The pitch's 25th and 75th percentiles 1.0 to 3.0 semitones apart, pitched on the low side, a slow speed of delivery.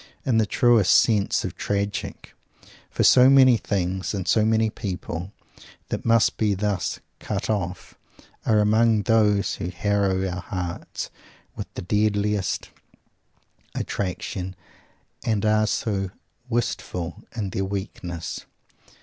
Yes: narrow, 2.6 semitones; low, 100 Hz; slow, 115 wpm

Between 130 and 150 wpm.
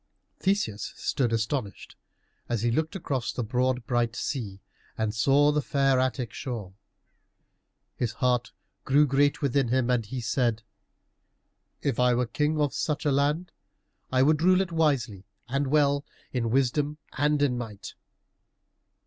Yes: average, 145 wpm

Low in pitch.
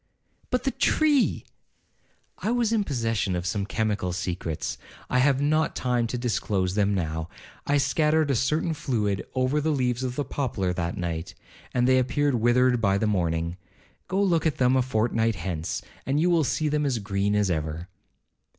Yes: low, 120 Hz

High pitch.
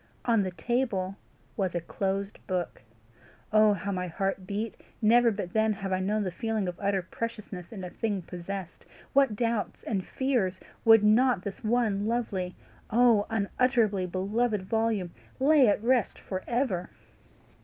Yes: high, 205 Hz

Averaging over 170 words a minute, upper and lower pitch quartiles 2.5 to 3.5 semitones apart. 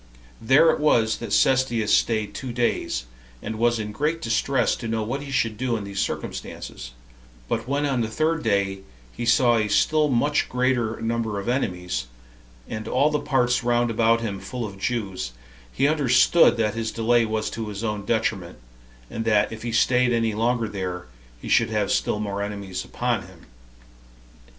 Yes: average, 180 wpm; average, 3.0 semitones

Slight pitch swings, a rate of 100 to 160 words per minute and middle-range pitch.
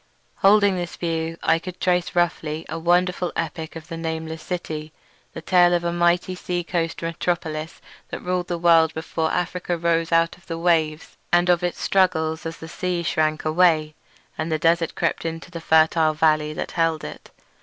No: narrow, 1.6 semitones; average, 185 wpm; medium, 165 Hz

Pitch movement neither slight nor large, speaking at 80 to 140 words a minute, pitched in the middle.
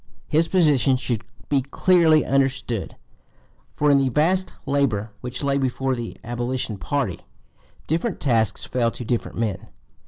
No: average, 3.5 semitones; slow, 135 wpm; low, 130 Hz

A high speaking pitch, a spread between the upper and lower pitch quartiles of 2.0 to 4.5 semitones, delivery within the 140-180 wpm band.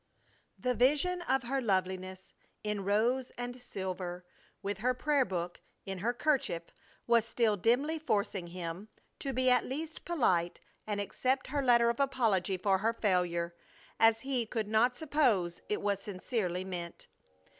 No: high, 220 Hz; average, 5.3 semitones; average, 150 wpm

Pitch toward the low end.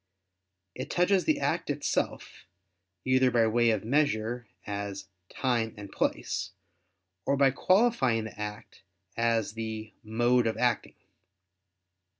Yes: low, 115 Hz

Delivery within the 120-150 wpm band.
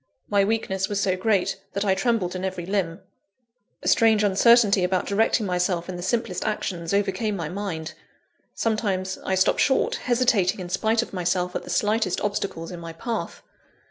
No: average, 175 wpm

